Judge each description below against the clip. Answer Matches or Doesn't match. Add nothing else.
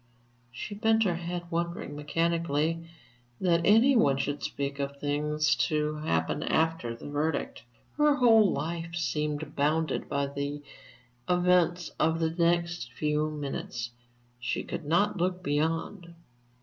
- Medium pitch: Matches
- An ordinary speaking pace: Doesn't match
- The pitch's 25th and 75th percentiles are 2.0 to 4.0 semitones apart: Matches